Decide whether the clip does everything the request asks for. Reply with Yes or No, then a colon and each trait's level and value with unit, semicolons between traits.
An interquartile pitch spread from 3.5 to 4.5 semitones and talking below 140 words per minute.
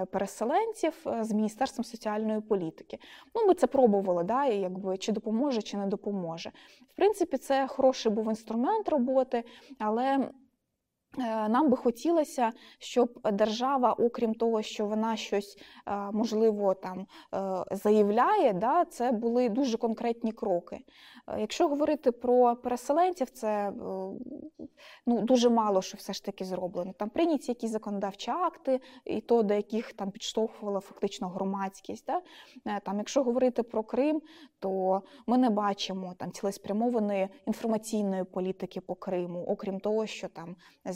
Yes: average, 4.2 semitones; average, 130 wpm